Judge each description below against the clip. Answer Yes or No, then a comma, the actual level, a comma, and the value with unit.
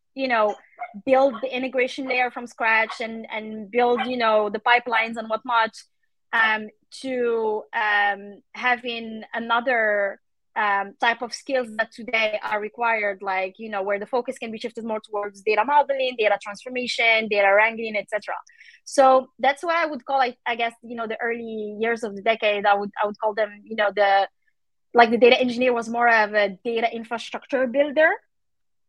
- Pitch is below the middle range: No, high, 230 Hz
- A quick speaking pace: No, average, 175 wpm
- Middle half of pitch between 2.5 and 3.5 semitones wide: Yes, average, 2.8 semitones